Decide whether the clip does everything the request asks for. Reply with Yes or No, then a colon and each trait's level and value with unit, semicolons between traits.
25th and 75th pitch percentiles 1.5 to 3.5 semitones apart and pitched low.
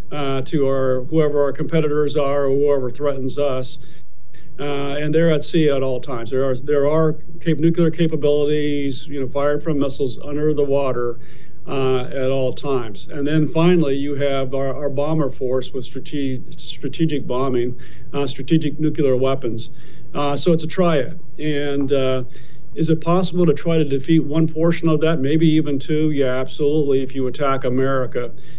No: narrow, 2.5 semitones; medium, 145 Hz